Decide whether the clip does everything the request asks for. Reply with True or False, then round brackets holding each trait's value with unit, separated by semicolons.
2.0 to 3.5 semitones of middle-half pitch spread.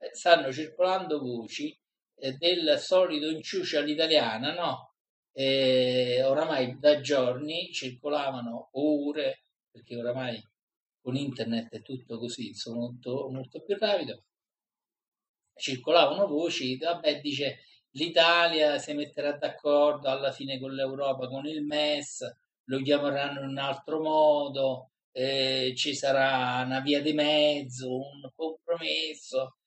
True (2.7 semitones)